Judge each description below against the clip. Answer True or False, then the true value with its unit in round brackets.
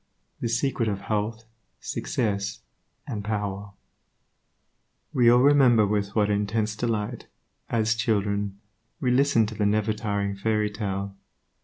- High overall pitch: False (105 Hz)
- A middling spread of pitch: False (1.9 semitones)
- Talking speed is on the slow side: True (120 wpm)